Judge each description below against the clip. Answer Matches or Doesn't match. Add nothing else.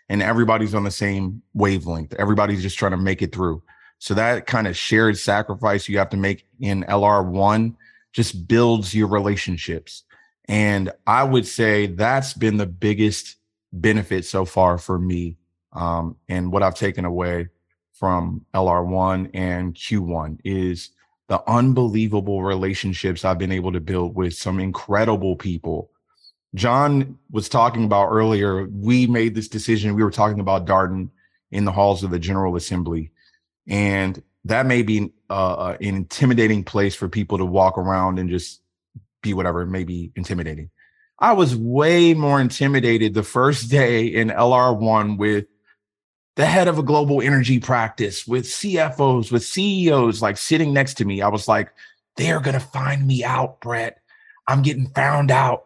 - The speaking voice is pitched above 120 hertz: Doesn't match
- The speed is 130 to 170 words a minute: Matches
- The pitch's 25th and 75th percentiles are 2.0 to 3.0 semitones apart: Doesn't match